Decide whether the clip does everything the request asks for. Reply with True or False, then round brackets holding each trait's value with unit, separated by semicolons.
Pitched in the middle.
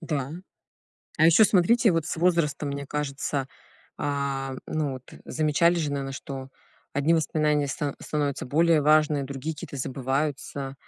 True (145 Hz)